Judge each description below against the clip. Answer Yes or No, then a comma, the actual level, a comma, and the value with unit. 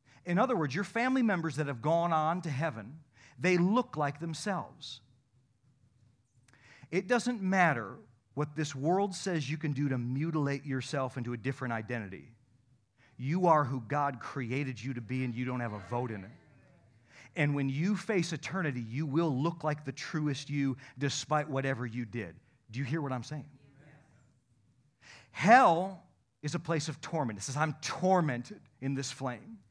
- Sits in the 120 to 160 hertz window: Yes, medium, 140 Hz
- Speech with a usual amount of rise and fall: Yes, average, 4.2 semitones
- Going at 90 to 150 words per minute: No, average, 170 wpm